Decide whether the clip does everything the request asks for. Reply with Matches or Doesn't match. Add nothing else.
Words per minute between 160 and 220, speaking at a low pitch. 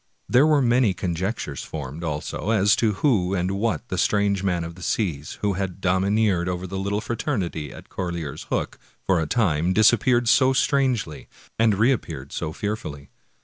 Matches